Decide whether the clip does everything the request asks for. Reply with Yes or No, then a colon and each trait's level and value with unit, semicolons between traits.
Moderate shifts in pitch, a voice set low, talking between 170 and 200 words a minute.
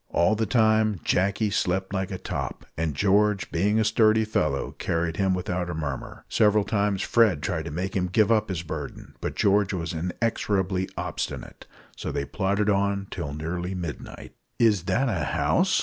Yes: average, 3.4 semitones; very low, 95 Hz; average, 175 wpm